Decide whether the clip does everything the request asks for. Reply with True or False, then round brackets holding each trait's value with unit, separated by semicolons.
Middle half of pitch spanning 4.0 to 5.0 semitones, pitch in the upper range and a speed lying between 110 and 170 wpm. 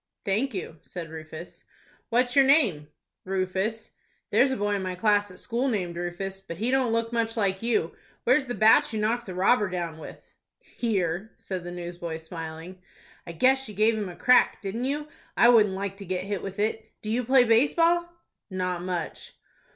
False (4.6 semitones; 205 Hz; 190 wpm)